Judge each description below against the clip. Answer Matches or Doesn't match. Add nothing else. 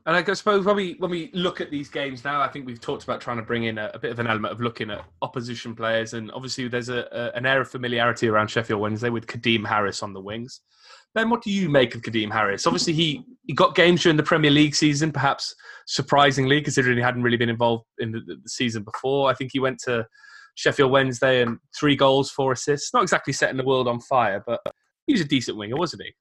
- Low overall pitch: Matches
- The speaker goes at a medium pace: Doesn't match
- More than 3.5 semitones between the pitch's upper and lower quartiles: Matches